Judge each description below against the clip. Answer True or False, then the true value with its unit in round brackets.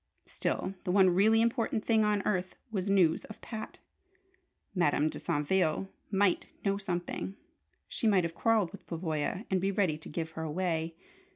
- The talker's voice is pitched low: False (185 Hz)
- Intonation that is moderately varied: True (3.7 semitones)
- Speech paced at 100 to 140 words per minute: False (165 wpm)